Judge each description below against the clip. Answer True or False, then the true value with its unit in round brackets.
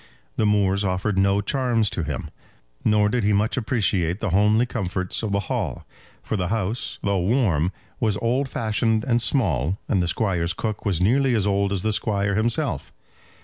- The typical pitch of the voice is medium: False (105 Hz)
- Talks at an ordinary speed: True (180 wpm)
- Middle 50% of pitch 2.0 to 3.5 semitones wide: True (3.0 semitones)